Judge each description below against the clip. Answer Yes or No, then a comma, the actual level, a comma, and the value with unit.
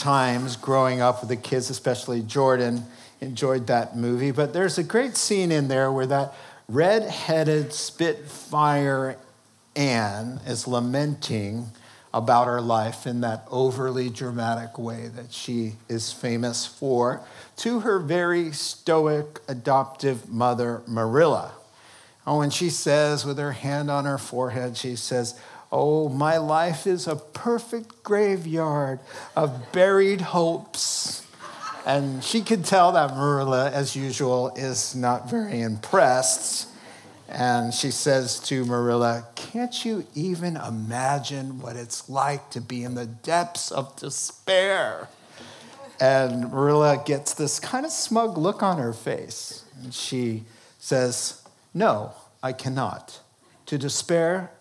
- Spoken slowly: Yes, slow, 130 wpm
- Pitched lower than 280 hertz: Yes, low, 135 Hz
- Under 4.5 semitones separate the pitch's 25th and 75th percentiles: Yes, average, 4.0 semitones